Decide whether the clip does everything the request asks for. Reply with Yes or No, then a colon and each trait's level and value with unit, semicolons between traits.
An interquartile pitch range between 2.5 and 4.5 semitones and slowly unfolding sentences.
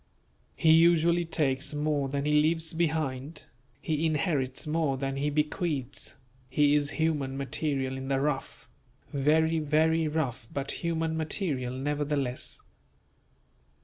Yes: average, 2.8 semitones; slow, 120 wpm